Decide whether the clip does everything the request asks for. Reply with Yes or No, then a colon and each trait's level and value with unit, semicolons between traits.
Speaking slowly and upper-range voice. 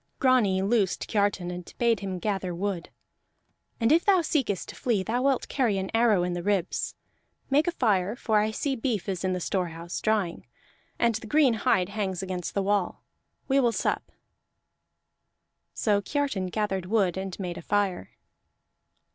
No: average, 165 wpm; high, 205 Hz